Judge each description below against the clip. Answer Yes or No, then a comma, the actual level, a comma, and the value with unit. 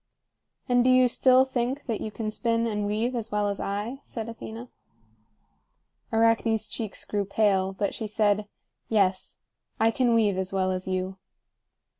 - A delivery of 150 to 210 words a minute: Yes, average, 160 wpm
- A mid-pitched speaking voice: No, high, 220 Hz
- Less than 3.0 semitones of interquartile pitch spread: Yes, narrow, 2.5 semitones